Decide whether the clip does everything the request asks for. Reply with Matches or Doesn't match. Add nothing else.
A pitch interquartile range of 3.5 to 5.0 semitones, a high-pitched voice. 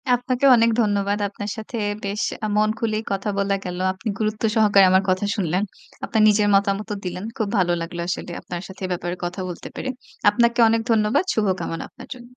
Doesn't match